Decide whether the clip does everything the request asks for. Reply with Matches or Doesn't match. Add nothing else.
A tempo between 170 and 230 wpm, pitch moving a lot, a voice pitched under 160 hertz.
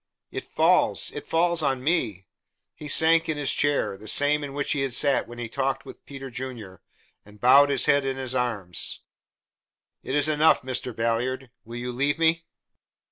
Doesn't match